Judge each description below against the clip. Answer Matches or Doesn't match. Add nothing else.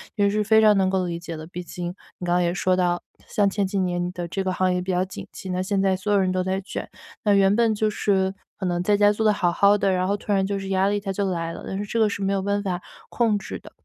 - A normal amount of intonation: Doesn't match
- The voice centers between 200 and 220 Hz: Doesn't match